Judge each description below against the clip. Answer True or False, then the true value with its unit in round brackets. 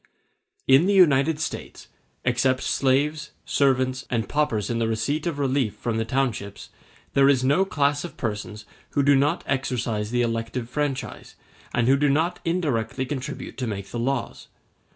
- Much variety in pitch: False (3.7 semitones)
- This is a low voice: True (130 Hz)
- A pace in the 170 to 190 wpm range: False (160 wpm)